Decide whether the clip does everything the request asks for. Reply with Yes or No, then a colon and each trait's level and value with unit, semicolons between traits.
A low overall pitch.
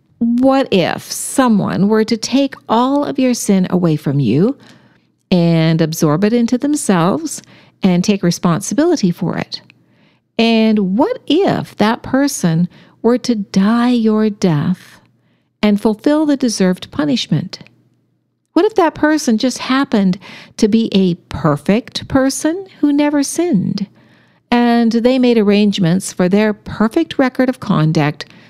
No: high, 220 Hz